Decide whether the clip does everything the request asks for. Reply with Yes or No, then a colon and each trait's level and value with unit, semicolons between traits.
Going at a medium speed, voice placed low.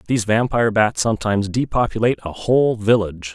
Yes: average, 145 wpm; low, 110 Hz